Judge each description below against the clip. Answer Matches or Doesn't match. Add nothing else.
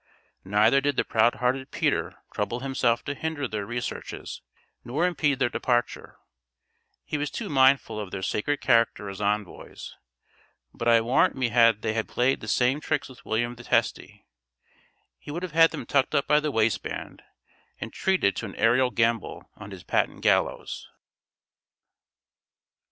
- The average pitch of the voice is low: Matches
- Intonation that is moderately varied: Matches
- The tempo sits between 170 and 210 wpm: Doesn't match